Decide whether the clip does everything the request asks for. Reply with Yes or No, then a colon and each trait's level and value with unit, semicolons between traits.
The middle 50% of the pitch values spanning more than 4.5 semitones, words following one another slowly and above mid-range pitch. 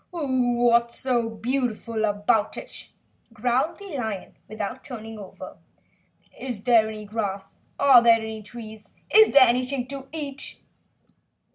No: average, 3.2 semitones; slow, 125 wpm; high, 235 Hz